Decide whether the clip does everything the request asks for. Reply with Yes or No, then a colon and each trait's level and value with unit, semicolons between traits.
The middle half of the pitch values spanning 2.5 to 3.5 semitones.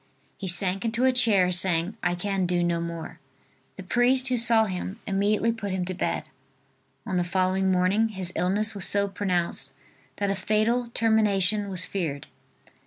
Yes: average, 3.1 semitones